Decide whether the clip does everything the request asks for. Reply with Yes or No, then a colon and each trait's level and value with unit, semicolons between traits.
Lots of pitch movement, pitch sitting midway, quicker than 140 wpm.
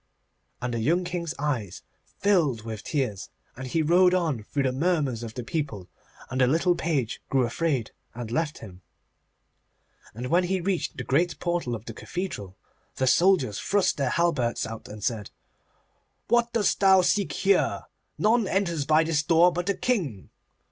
Yes: wide, 6.6 semitones; medium, 155 Hz; average, 170 wpm